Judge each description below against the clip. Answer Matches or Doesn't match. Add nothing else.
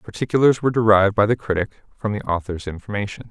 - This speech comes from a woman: Doesn't match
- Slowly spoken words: Doesn't match